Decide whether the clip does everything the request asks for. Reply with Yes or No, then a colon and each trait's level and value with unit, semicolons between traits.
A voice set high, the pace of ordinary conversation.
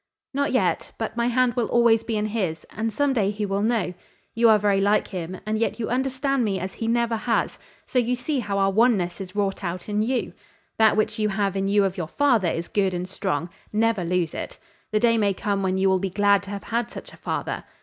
No: high, 210 Hz; fast, 240 wpm